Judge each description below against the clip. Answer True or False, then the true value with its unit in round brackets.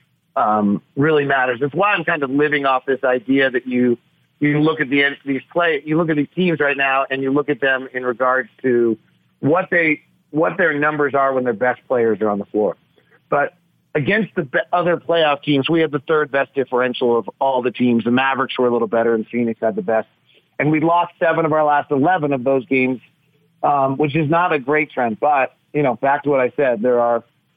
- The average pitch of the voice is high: False (135 Hz)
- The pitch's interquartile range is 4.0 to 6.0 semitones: False (3.3 semitones)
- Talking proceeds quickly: True (225 wpm)